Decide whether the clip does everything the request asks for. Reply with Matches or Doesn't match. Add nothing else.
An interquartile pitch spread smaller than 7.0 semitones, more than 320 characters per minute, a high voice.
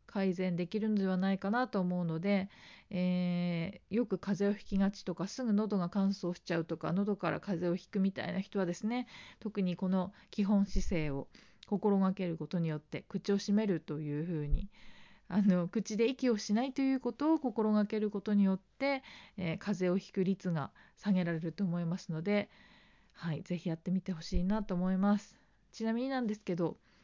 Matches